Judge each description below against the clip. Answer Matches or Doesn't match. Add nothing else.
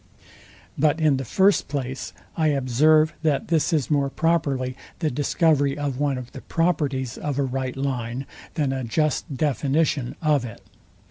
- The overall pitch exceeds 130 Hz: Matches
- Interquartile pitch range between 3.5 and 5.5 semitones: Doesn't match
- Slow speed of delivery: Doesn't match